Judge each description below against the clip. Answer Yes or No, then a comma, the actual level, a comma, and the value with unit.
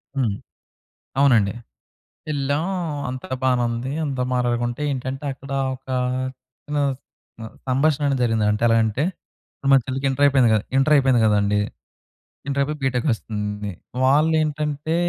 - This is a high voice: No, low, 130 Hz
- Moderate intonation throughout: Yes, average, 3.3 semitones